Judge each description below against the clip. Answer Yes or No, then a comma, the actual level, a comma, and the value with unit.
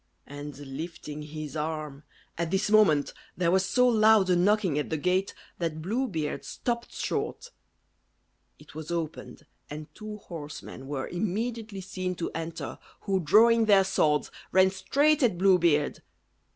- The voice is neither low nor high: Yes, medium, 180 Hz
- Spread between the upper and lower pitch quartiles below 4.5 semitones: No, wide, 5.5 semitones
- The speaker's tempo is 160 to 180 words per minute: No, average, 150 wpm